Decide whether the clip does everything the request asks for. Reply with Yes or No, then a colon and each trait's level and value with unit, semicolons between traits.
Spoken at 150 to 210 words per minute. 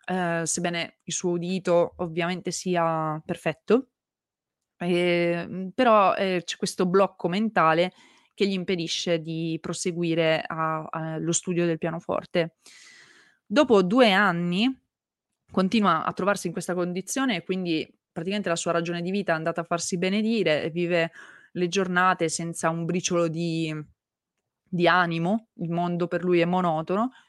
No: average, 135 wpm